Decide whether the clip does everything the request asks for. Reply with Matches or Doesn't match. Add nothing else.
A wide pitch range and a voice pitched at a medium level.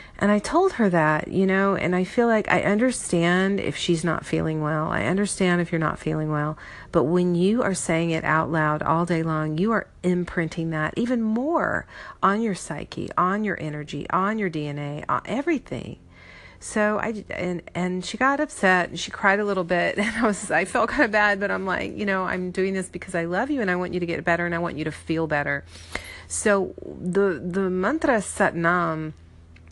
Doesn't match